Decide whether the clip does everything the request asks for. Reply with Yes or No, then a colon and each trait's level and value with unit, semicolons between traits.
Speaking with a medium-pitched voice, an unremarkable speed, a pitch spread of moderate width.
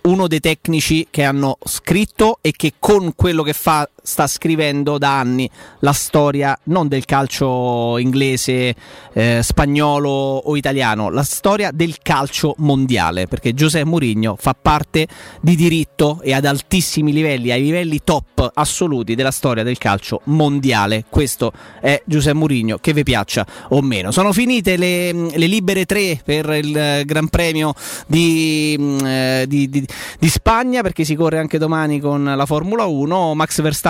Yes: medium, 150 Hz; average, 155 wpm; average, 3.4 semitones